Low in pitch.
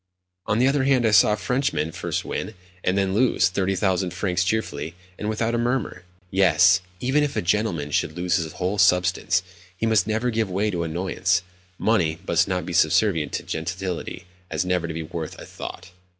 Yes: very low, 95 Hz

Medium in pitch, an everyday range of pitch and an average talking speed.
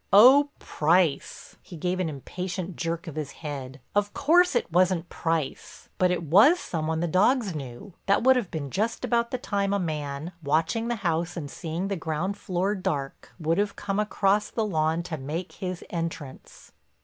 Yes: medium, 175 Hz; average, 4.2 semitones; average, 180 wpm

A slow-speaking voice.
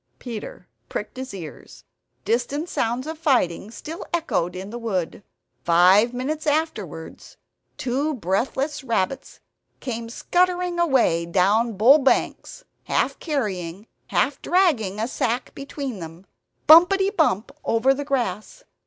Yes: slow, 120 wpm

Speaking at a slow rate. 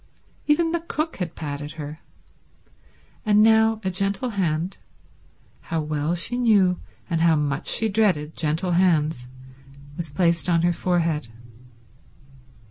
Yes: slow, 120 wpm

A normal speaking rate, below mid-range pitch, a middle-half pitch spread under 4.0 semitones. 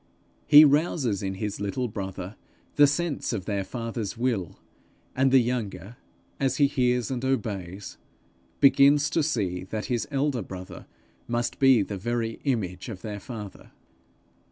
No: average, 145 wpm; low, 115 Hz; average, 5.2 semitones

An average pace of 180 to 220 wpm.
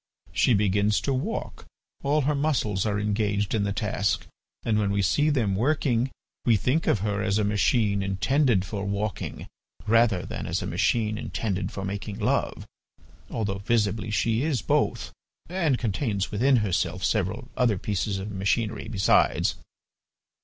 No: average, 155 wpm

